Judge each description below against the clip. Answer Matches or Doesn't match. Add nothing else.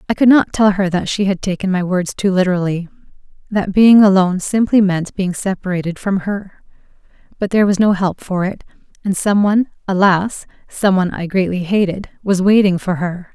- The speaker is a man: Doesn't match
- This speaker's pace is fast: Doesn't match